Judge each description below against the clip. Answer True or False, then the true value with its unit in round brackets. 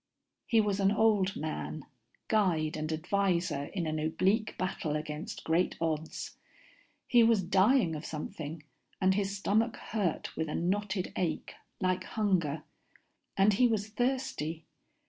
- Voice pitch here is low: False (185 Hz)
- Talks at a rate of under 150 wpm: True (135 wpm)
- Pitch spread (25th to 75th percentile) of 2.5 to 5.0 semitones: True (4.7 semitones)